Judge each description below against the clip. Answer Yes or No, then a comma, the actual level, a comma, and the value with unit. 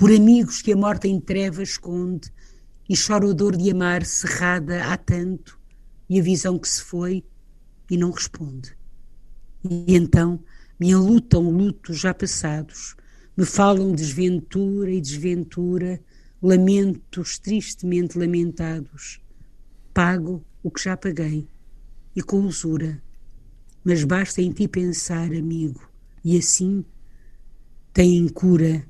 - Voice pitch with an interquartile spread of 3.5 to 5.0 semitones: No, average, 2.8 semitones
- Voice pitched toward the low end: No, medium, 175 Hz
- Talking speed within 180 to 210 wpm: No, average, 125 wpm